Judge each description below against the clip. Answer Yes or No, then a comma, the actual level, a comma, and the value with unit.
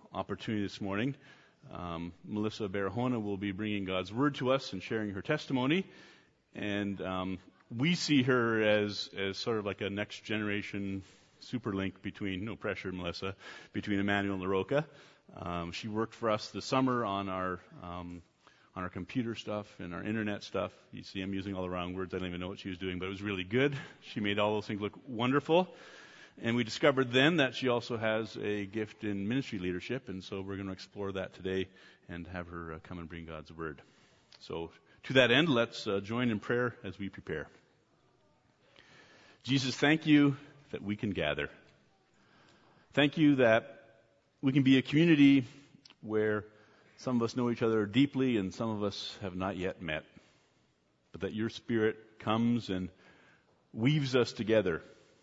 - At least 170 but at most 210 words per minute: Yes, average, 180 wpm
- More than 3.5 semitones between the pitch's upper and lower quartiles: Yes, average, 4.5 semitones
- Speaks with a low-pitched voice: Yes, low, 105 Hz